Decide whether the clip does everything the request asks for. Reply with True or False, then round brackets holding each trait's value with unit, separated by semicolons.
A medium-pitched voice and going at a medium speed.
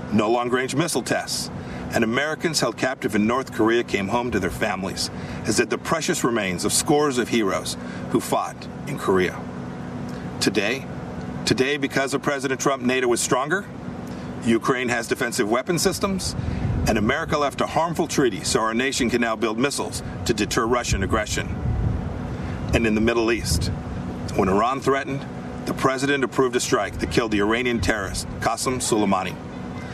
False (115 Hz; 160 wpm)